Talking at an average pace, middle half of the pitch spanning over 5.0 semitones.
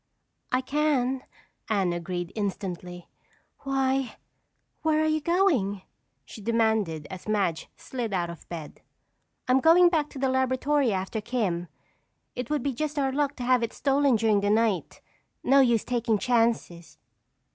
Yes: average, 145 wpm; wide, 5.6 semitones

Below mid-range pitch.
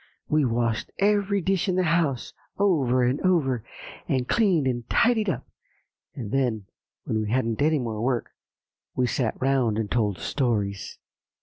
Yes: low, 130 Hz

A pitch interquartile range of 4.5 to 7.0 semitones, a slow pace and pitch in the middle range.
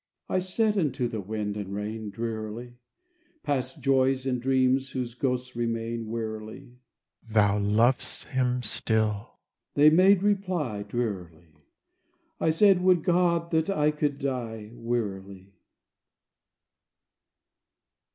No: average, 5.1 semitones; slow, 110 wpm; low, 125 Hz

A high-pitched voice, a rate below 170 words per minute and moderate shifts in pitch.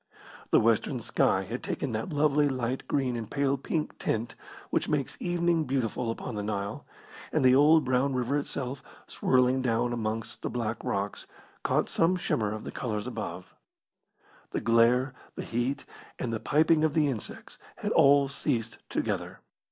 No: low, 125 Hz; average, 160 wpm; average, 3.7 semitones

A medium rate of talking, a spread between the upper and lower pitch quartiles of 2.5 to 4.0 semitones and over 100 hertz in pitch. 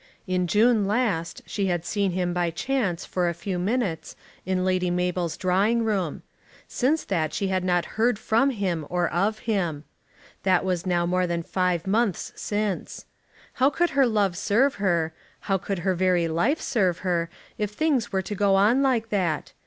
Yes: average, 175 wpm; average, 3.5 semitones; high, 190 Hz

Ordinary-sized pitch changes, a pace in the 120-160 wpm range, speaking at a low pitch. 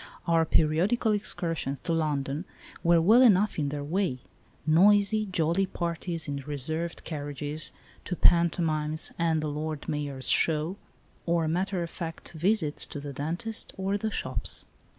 No: average, 3.7 semitones; average, 140 wpm; medium, 165 Hz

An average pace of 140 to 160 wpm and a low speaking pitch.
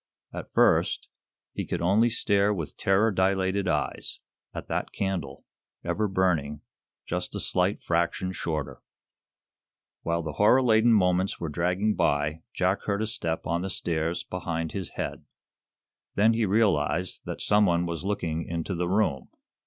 Yes: average, 150 wpm; very low, 90 Hz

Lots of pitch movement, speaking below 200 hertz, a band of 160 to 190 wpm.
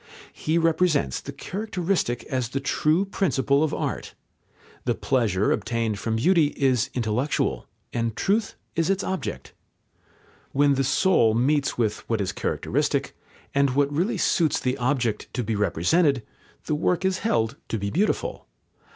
No: wide, 6.3 semitones; medium, 140 Hz; average, 145 wpm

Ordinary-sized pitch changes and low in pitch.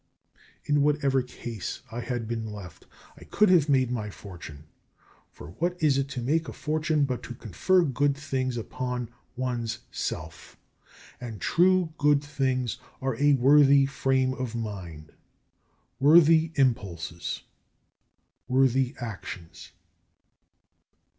Yes: average, 4.0 semitones; low, 130 Hz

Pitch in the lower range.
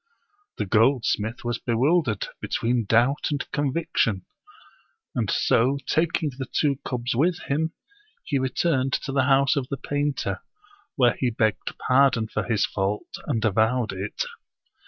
Yes: low, 130 Hz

